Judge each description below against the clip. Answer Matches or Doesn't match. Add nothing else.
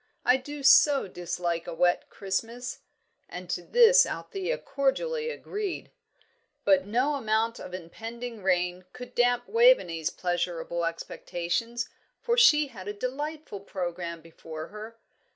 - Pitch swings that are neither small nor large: Doesn't match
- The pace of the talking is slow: Matches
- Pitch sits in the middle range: Doesn't match